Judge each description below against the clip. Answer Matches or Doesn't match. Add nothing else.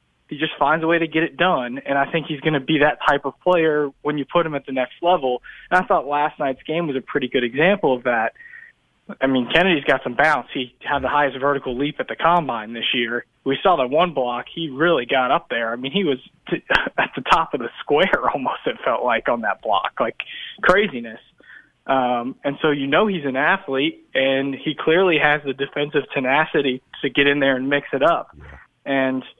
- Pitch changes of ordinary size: Matches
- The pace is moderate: Doesn't match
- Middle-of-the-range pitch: Matches